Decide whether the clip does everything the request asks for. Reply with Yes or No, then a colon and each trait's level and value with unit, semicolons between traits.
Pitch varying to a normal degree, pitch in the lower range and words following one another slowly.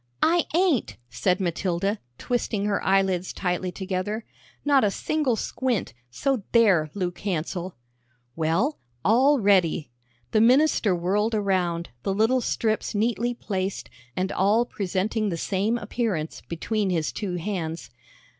No: average, 4.2 semitones; high, 200 Hz; slow, 125 wpm